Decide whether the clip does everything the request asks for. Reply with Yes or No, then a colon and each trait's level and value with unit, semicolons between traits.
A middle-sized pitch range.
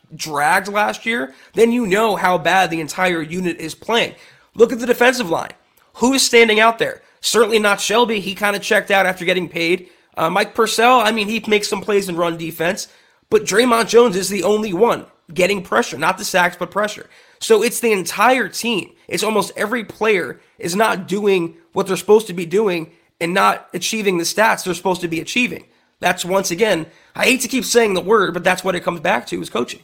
Yes: average, 4.0 semitones